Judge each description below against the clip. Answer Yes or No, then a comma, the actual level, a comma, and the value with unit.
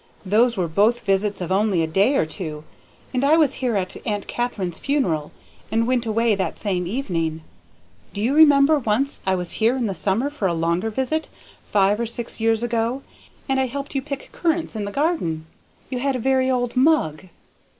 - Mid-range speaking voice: No, high, 225 Hz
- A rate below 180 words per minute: No, average, 195 wpm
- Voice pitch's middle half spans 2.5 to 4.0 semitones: No, wide, 5.6 semitones